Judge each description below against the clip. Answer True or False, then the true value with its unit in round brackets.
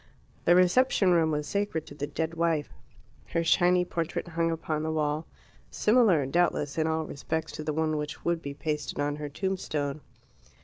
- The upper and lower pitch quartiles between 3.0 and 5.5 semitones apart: False (2.4 semitones)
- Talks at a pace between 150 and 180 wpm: True (175 wpm)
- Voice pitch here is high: False (160 Hz)